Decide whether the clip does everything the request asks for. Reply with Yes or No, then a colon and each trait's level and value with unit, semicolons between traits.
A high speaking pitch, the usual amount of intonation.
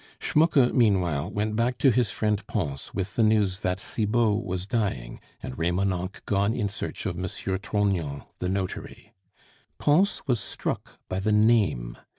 No: low, 100 Hz; average, 3.4 semitones